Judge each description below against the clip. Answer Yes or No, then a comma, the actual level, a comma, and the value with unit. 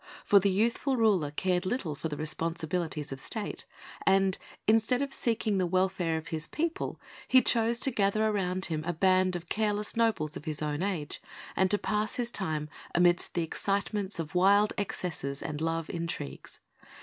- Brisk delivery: No, average, 175 wpm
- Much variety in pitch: No, average, 4.5 semitones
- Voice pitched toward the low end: No, medium, 185 Hz